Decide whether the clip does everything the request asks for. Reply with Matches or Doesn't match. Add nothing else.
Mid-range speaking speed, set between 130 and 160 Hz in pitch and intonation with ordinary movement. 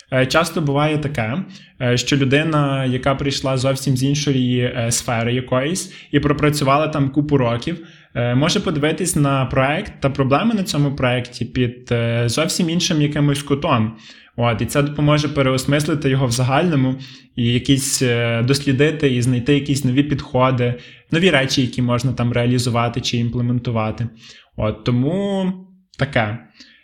Matches